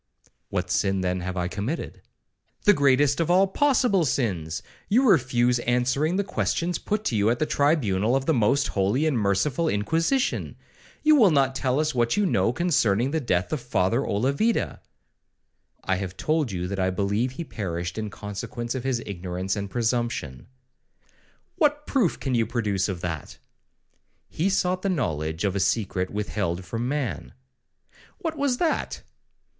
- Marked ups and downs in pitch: Yes, wide, 8.4 semitones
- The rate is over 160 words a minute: No, average, 155 wpm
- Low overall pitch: Yes, low, 120 Hz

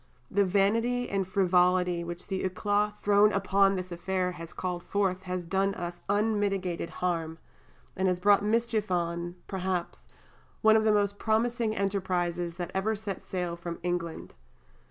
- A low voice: No, high, 190 Hz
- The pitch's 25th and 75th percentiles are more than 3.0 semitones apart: No, narrow, 2.5 semitones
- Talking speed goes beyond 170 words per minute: No, average, 150 wpm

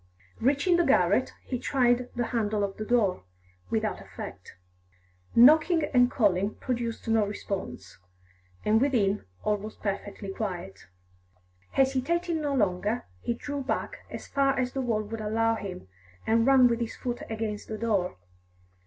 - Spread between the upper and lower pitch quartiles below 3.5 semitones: No, average, 3.9 semitones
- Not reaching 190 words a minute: Yes, average, 145 wpm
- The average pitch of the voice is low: No, high, 230 Hz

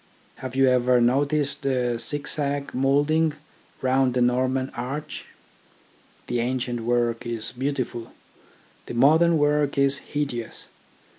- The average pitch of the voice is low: Yes, low, 130 Hz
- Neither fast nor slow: No, slow, 120 wpm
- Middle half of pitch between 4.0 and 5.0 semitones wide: No, average, 2.7 semitones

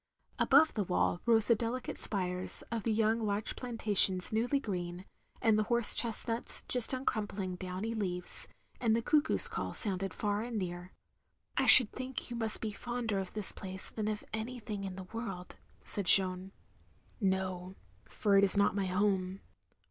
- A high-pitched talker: Yes, high, 210 Hz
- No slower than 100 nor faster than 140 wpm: No, average, 165 wpm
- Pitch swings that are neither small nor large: Yes, average, 3.3 semitones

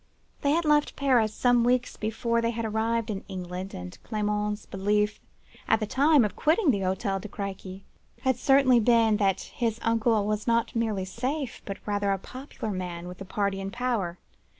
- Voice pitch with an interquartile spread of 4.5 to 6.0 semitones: No, average, 3.6 semitones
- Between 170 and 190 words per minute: Yes, average, 180 wpm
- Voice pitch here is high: Yes, high, 215 Hz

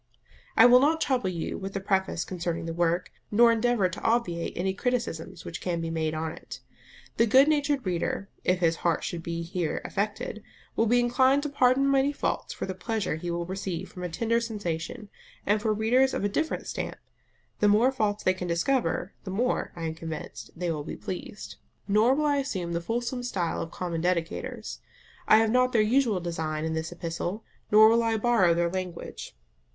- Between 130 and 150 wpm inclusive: No, average, 200 wpm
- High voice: Yes, high, 195 Hz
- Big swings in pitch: Yes, wide, 5.8 semitones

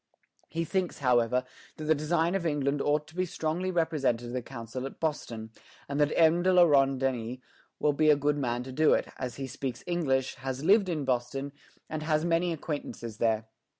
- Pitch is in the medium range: Yes, medium, 145 Hz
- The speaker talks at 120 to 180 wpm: No, fast, 205 wpm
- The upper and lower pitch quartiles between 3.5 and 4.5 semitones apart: Yes, average, 4.2 semitones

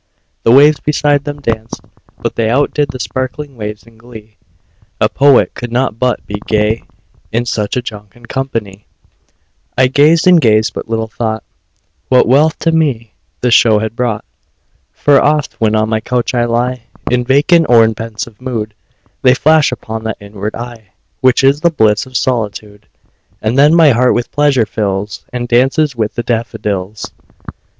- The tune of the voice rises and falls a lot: No, average, 3.6 semitones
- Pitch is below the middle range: Yes, low, 120 Hz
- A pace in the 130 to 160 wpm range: No, average, 170 wpm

